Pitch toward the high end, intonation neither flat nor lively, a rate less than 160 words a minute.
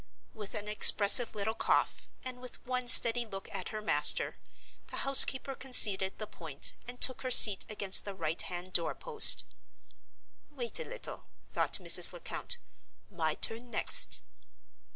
Yes: high, 220 Hz; average, 4.5 semitones; average, 150 wpm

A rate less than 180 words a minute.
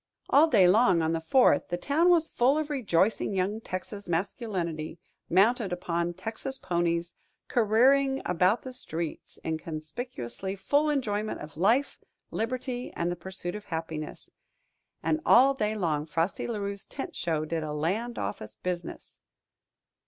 Yes: average, 145 wpm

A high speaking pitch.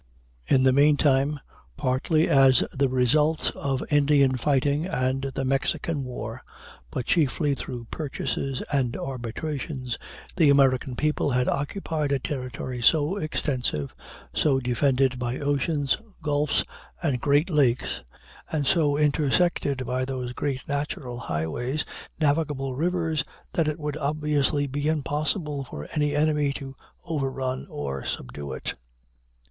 No: medium, 140 Hz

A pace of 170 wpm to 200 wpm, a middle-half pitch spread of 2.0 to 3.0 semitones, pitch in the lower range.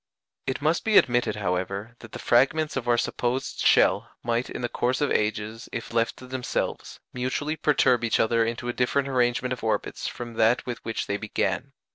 Yes: average, 190 wpm; narrow, 2.4 semitones; low, 120 Hz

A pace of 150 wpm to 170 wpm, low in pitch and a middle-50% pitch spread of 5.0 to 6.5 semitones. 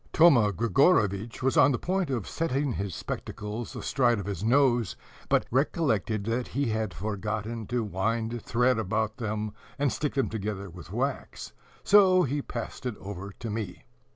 No: average, 160 wpm; low, 115 Hz; average, 4.1 semitones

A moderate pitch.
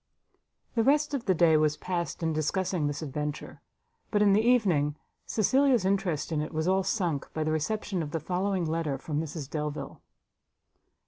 Yes: medium, 165 Hz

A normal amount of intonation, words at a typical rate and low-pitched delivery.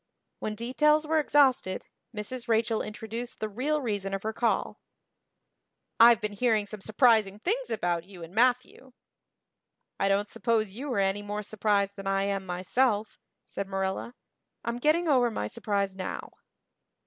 No: average, 3.8 semitones; average, 150 wpm; high, 215 Hz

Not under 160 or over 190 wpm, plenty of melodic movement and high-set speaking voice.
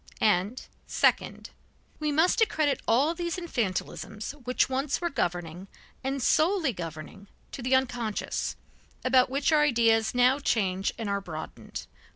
No: slow, 135 wpm; wide, 6.4 semitones; very high, 250 Hz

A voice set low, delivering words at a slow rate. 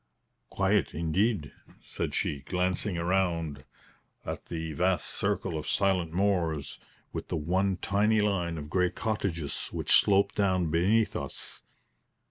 Yes: very low, 90 Hz; slow, 125 wpm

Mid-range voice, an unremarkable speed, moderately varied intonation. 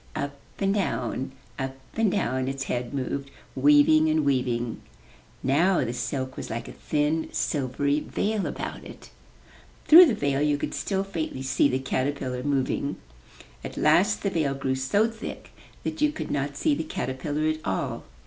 Yes: medium, 145 Hz; average, 165 wpm; average, 3.3 semitones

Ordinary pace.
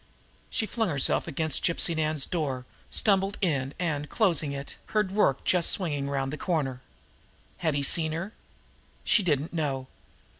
Yes: average, 150 wpm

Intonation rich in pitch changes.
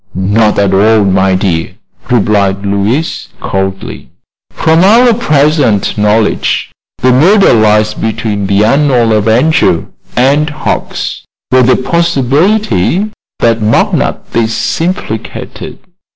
Yes: wide, 6.9 semitones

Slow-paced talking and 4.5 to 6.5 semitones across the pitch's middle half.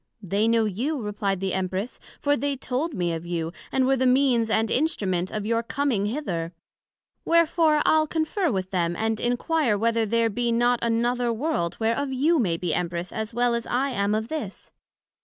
No: average, 185 wpm; average, 5.2 semitones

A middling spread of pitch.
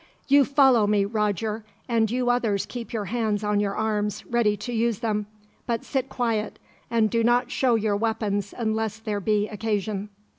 No: narrow, 2.2 semitones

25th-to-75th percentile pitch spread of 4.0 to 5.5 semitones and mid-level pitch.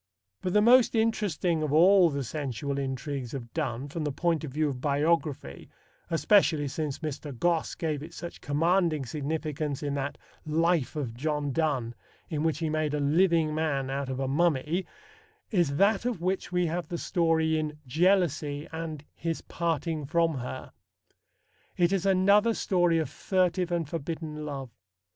No: average, 3.3 semitones; medium, 155 Hz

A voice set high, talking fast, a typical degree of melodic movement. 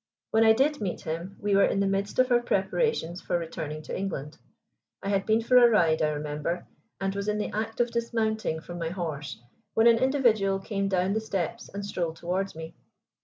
Yes: high, 195 Hz; fast, 210 wpm; average, 4.6 semitones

